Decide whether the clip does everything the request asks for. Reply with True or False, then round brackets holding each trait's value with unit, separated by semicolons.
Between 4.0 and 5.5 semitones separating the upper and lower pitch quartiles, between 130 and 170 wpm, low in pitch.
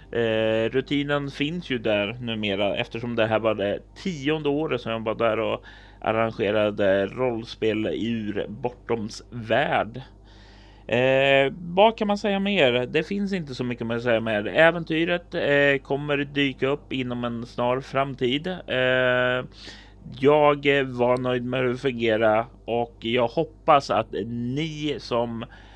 True (4.3 semitones; 140 wpm; 125 Hz)